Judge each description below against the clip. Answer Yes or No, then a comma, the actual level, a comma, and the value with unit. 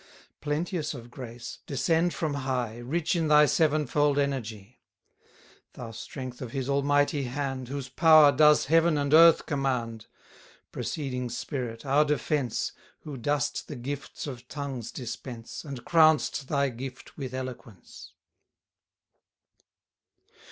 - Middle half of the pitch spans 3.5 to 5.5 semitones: No, average, 3.1 semitones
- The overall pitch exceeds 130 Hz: Yes, medium, 140 Hz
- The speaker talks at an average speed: No, slow, 120 wpm